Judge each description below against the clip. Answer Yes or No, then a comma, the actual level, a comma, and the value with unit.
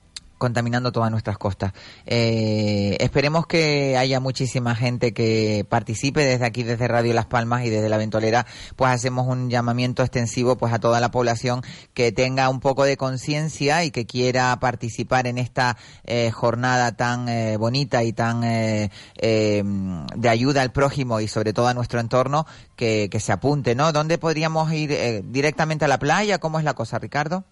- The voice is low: Yes, low, 125 Hz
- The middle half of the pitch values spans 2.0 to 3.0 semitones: Yes, average, 2.7 semitones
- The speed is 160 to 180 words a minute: Yes, average, 175 wpm